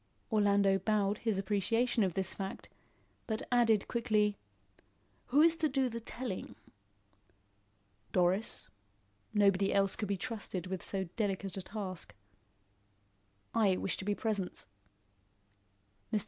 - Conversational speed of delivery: No, slow, 120 wpm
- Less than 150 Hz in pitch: No, high, 205 Hz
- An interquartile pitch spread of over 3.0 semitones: No, average, 2.7 semitones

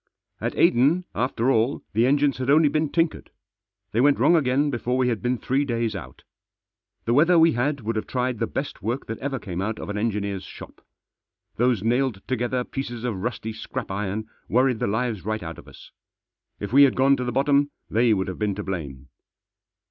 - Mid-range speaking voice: No, low, 120 Hz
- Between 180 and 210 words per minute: Yes, average, 200 wpm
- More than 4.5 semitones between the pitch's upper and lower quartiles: No, average, 3.9 semitones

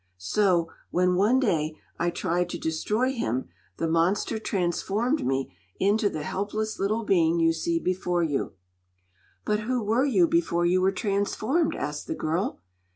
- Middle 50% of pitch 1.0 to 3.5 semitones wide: No, average, 4.5 semitones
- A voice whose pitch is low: No, medium, 185 Hz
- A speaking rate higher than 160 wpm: No, average, 155 wpm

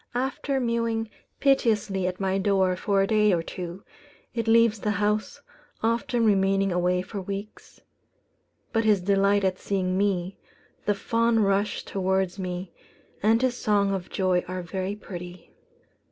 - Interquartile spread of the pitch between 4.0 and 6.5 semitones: No, average, 2.8 semitones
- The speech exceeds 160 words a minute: No, average, 145 wpm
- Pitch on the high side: Yes, high, 200 Hz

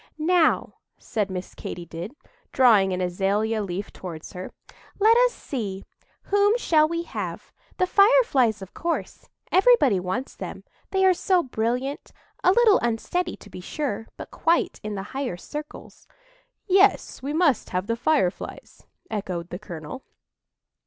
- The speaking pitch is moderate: No, very high, 250 Hz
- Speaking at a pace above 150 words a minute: No, average, 140 wpm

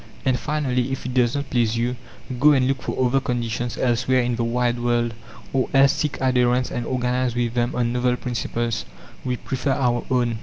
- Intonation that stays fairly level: Yes, narrow, 1.3 semitones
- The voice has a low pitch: Yes, low, 125 Hz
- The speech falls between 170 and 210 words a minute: Yes, average, 195 wpm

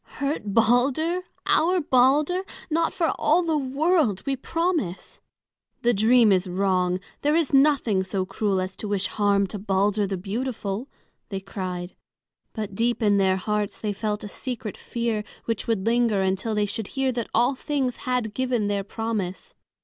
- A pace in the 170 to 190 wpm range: No, average, 160 wpm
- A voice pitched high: Yes, high, 220 Hz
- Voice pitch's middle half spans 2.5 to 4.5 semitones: No, average, 4.9 semitones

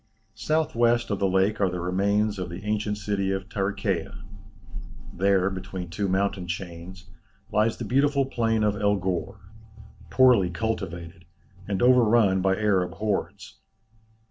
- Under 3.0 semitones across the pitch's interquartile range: Yes, narrow, 2.4 semitones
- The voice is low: Yes, low, 100 Hz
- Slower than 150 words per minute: Yes, average, 140 wpm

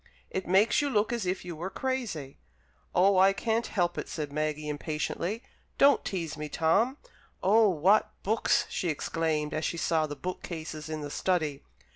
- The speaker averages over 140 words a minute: Yes, average, 175 wpm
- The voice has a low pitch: No, medium, 175 Hz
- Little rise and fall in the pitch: No, average, 4.9 semitones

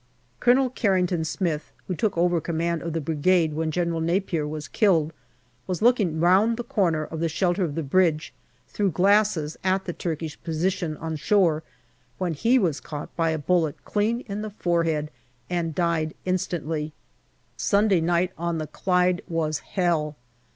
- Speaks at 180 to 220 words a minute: No, average, 160 wpm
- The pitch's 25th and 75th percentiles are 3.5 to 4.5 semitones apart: No, average, 2.9 semitones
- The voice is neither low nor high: Yes, medium, 170 Hz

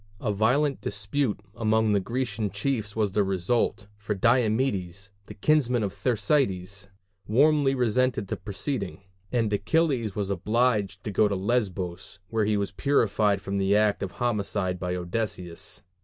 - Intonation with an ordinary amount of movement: Yes, average, 3.7 semitones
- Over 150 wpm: No, average, 145 wpm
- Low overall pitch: Yes, low, 105 Hz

